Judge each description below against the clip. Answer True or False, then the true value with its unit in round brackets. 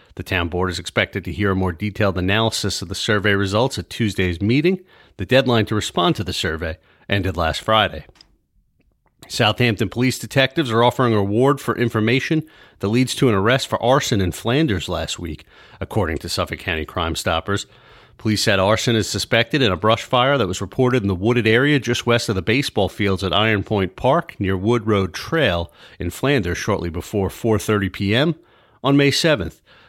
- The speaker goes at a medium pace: True (185 wpm)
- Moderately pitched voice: False (105 Hz)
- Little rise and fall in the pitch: False (4.2 semitones)